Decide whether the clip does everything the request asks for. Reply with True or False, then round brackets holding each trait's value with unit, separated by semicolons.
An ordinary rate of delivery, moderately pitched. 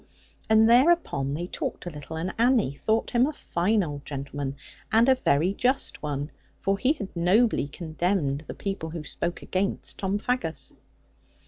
True (160 wpm; 180 Hz)